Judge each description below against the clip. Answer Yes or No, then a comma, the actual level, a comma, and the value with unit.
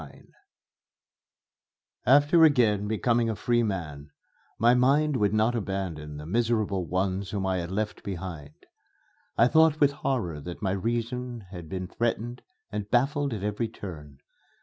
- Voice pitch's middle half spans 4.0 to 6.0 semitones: Yes, average, 4.6 semitones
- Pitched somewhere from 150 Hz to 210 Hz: No, low, 105 Hz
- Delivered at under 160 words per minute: Yes, average, 145 wpm